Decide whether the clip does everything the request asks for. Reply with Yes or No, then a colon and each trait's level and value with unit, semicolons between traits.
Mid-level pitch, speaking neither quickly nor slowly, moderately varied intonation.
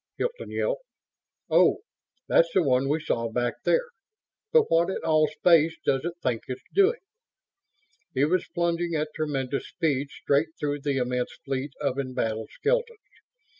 Yes: medium, 150 Hz; average, 150 wpm; average, 4.5 semitones